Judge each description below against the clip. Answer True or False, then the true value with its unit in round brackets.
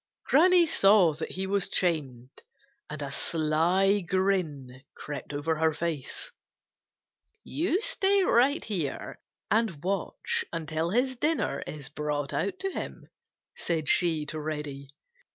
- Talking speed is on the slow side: True (125 wpm)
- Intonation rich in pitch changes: True (6.0 semitones)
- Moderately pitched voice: True (165 Hz)